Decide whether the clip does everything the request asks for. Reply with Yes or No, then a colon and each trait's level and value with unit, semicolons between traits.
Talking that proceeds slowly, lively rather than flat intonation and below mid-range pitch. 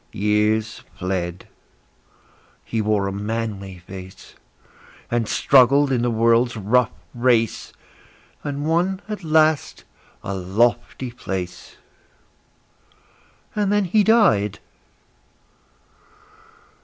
Yes: slow, 90 wpm; wide, 6.1 semitones; low, 115 Hz